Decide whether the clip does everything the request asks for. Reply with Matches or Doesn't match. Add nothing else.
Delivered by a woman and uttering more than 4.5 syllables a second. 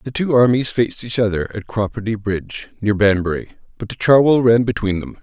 Doesn't match